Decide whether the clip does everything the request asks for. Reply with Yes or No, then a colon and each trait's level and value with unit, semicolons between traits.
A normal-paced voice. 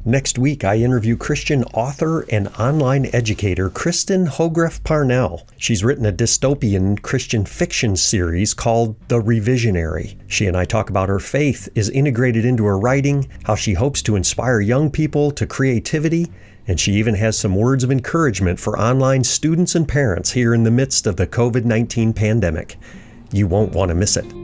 Yes: average, 170 wpm